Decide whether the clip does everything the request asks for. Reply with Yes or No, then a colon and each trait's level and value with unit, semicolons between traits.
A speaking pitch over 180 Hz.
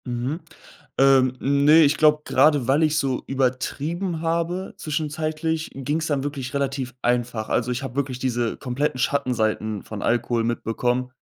No: low, 135 Hz